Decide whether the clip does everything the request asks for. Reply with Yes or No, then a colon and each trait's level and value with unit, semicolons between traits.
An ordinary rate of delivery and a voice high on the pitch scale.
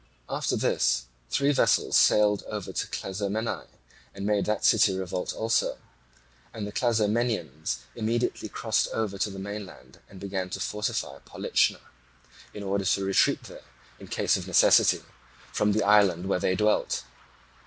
No: average, 145 wpm; low, 100 Hz